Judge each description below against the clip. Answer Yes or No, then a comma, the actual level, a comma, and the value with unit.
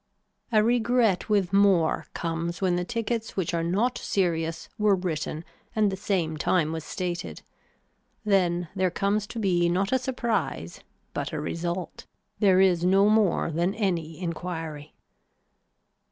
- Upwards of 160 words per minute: No, average, 140 wpm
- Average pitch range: Yes, average, 3.4 semitones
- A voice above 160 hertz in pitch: Yes, medium, 185 Hz